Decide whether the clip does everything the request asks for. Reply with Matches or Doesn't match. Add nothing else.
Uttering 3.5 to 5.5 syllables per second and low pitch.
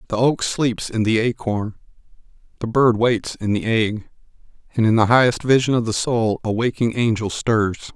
Matches